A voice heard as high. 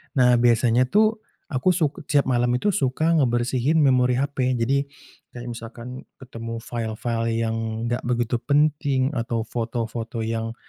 No: low, 125 Hz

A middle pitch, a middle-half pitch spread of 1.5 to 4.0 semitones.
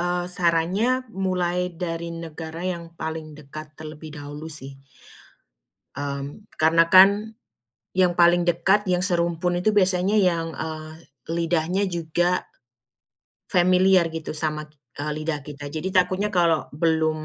Yes: medium, 170 Hz; narrow, 2.5 semitones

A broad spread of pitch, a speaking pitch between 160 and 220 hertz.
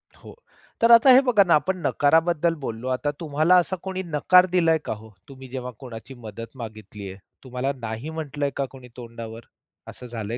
No: wide, 6.3 semitones; low, 135 Hz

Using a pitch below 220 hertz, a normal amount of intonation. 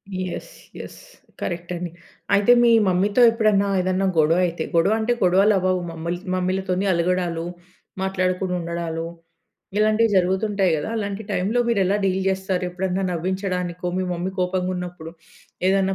No: medium, 185 Hz; narrow, 1.8 semitones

